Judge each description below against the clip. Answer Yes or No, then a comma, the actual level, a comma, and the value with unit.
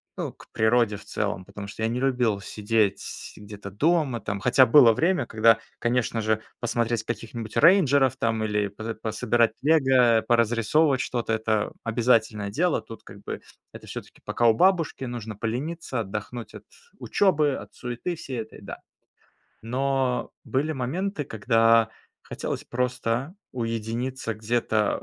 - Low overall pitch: Yes, low, 115 Hz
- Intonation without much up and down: No, average, 3.1 semitones